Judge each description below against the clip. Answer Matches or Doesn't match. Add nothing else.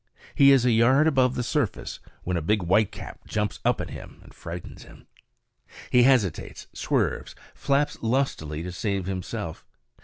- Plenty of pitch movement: Matches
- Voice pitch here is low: Matches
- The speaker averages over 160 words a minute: Doesn't match